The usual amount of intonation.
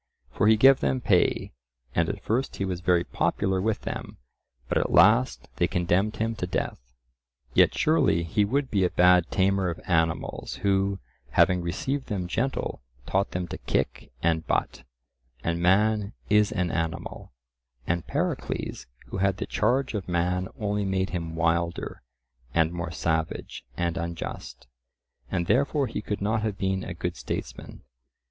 Yes: average, 3.6 semitones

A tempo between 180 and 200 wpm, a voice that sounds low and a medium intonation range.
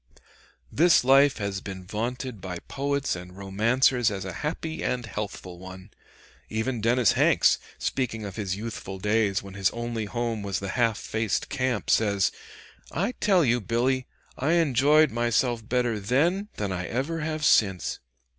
No: average, 155 wpm; low, 115 Hz; average, 4.8 semitones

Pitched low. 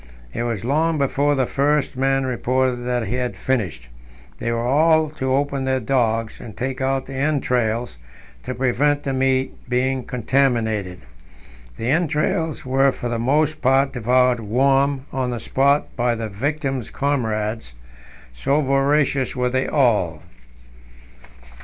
Yes: low, 130 Hz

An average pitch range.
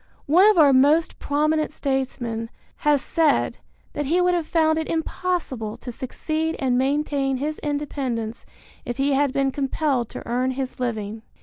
Yes: average, 3.4 semitones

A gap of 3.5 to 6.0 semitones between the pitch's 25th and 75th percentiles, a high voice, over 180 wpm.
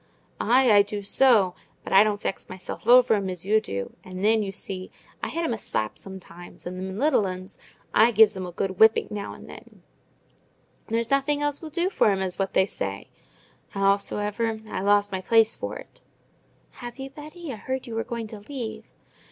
Yes: average, 4.0 semitones; high, 210 Hz; average, 200 wpm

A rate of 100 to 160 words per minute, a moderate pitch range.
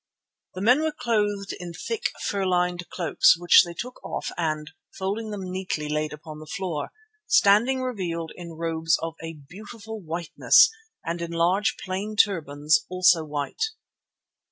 Yes: average, 150 wpm; average, 4.1 semitones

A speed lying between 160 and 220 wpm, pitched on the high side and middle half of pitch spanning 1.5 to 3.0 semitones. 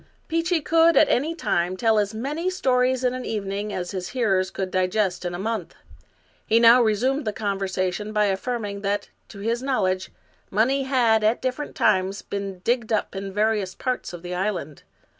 No: average, 180 wpm; high, 215 Hz; average, 4.6 semitones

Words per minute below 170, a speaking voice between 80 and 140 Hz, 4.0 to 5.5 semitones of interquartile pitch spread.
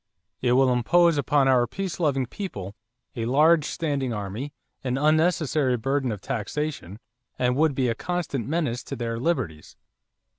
Yes: average, 150 wpm; low, 135 Hz; average, 4.4 semitones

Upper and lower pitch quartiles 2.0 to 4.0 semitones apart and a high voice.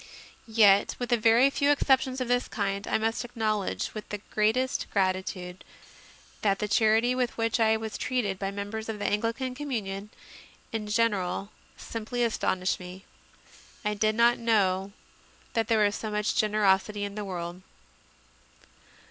Yes: narrow, 2.6 semitones; high, 215 Hz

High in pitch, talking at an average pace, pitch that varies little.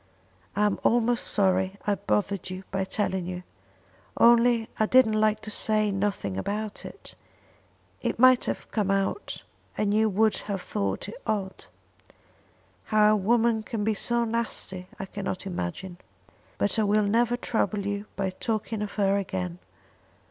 Yes: high, 205 Hz; average, 155 wpm; narrow, 2.3 semitones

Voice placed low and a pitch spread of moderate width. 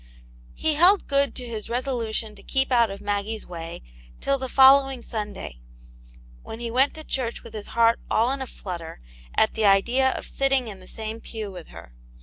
No: high, 230 Hz; average, 4.4 semitones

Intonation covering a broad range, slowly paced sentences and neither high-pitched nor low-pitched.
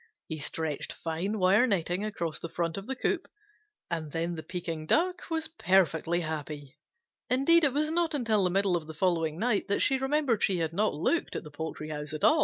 No: wide, 7.7 semitones; fast, 205 wpm; medium, 180 Hz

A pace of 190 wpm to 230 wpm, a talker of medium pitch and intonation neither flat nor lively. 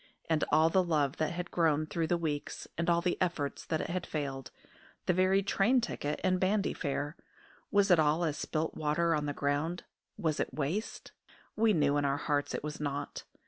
Yes: average, 195 wpm; medium, 160 Hz; average, 3.3 semitones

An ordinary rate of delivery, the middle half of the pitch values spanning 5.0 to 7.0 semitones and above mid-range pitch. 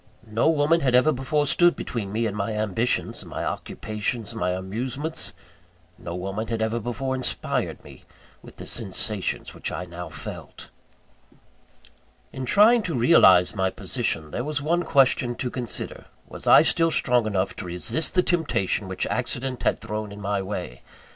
No: average, 165 wpm; wide, 5.6 semitones; low, 115 Hz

